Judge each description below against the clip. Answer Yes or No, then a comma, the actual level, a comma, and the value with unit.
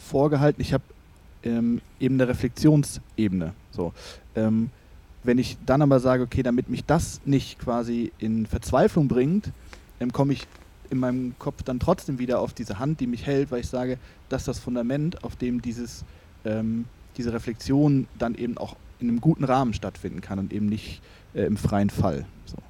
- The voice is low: Yes, low, 120 Hz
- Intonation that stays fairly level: No, average, 3.4 semitones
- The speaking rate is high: No, average, 180 wpm